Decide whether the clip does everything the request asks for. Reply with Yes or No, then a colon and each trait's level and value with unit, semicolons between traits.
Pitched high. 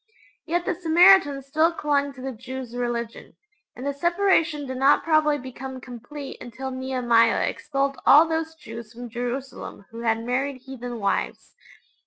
Yes: very high, 265 Hz